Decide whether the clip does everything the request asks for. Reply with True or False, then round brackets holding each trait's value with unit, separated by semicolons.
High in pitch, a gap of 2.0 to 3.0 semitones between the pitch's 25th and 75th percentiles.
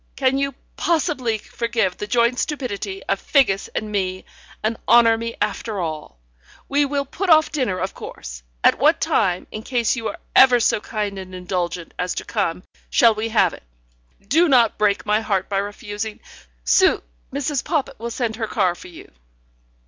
False (220 Hz; 4.5 semitones)